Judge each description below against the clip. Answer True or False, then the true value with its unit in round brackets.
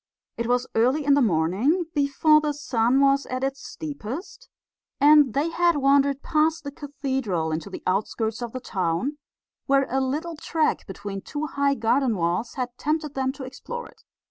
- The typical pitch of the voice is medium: False (275 Hz)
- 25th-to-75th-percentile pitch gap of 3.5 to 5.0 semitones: True (4.5 semitones)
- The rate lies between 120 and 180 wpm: True (170 wpm)